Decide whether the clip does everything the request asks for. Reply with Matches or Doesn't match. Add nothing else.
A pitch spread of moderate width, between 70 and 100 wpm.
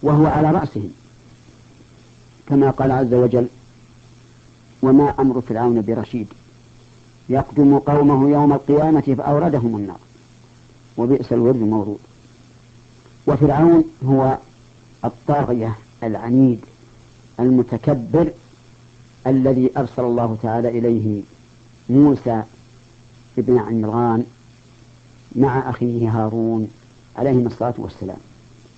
Doesn't match